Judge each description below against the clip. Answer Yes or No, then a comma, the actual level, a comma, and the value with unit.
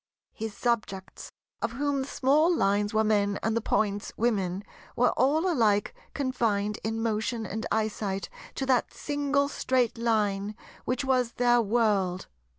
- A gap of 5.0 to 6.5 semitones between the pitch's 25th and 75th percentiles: No, average, 3.9 semitones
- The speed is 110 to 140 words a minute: Yes, slow, 135 wpm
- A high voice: Yes, high, 225 Hz